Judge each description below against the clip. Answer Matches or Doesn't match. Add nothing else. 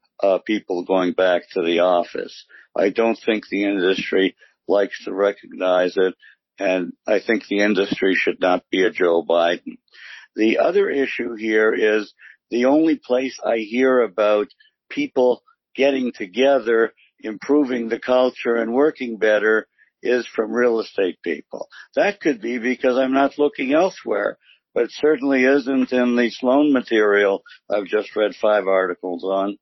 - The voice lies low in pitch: Matches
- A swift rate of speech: Doesn't match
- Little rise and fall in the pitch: Doesn't match